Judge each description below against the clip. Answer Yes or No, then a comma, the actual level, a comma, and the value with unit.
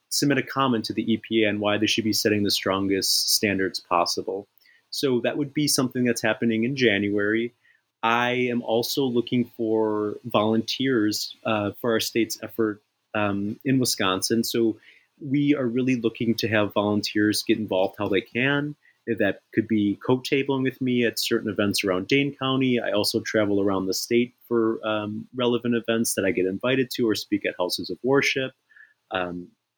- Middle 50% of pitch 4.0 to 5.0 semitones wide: No, average, 3.0 semitones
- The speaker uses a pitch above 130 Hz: No, low, 115 Hz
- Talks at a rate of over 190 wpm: No, average, 175 wpm